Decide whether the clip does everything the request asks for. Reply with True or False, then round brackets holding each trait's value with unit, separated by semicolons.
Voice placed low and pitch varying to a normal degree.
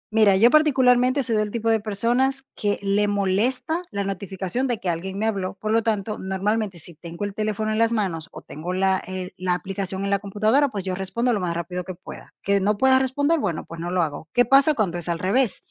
False (205 Hz; 3.7 semitones)